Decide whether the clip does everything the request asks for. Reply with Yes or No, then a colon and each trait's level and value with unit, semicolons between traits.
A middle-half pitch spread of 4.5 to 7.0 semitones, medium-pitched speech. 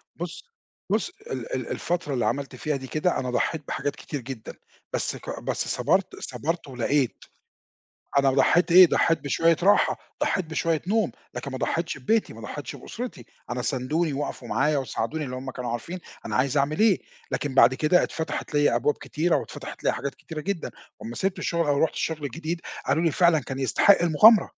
No: average, 4.1 semitones; medium, 150 Hz